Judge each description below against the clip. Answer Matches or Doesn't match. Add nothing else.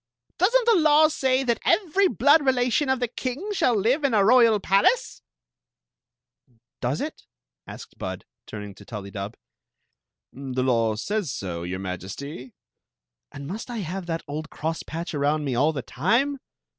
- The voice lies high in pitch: Matches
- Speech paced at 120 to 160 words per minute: Matches